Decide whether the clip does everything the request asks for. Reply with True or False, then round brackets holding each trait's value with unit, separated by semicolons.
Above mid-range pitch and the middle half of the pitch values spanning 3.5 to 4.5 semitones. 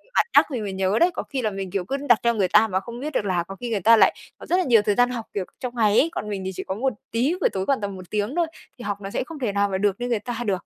True (215 Hz; 3.8 semitones)